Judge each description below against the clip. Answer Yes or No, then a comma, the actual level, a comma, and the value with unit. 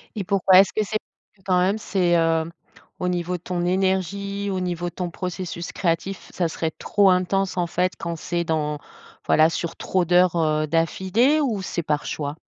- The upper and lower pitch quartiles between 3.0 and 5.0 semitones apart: No, narrow, 2.4 semitones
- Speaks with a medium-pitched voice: Yes, medium, 180 Hz